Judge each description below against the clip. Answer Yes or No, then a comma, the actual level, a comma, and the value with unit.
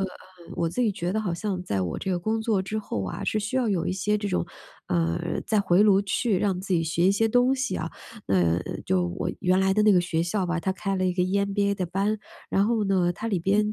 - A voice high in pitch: Yes, high, 195 Hz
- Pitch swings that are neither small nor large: Yes, average, 3.2 semitones